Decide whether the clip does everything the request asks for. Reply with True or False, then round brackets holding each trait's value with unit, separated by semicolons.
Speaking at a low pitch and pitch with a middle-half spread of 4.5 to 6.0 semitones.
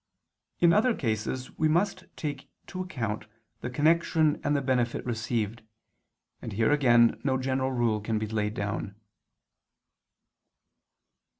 True (125 Hz; 5.1 semitones)